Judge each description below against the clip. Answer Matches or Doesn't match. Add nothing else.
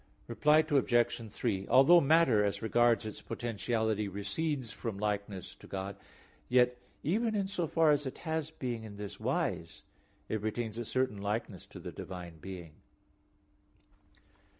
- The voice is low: Matches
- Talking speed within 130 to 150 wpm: Matches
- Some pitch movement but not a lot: Doesn't match